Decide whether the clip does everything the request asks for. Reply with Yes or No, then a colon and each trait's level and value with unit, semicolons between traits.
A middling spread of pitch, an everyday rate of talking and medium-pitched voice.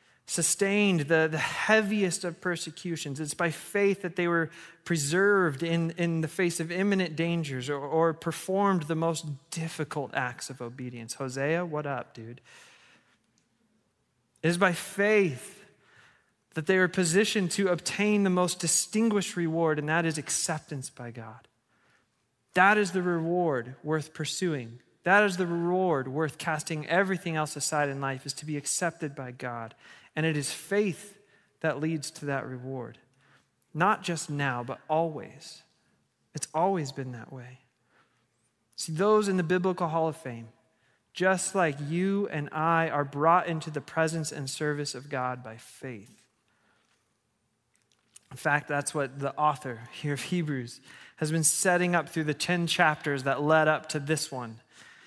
Yes: average, 4.4 semitones; average, 155 wpm; medium, 160 Hz